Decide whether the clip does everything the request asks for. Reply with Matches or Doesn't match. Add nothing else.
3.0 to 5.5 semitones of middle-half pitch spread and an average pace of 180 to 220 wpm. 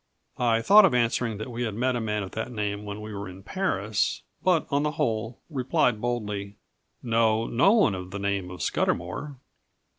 Matches